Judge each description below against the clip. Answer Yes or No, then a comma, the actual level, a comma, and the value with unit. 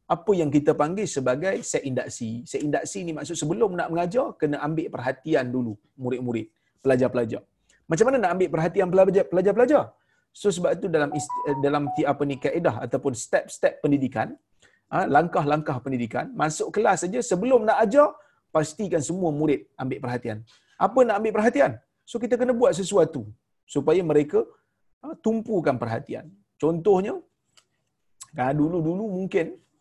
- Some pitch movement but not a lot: No, wide, 7.0 semitones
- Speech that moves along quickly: Yes, fast, 140 wpm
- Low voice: No, medium, 160 Hz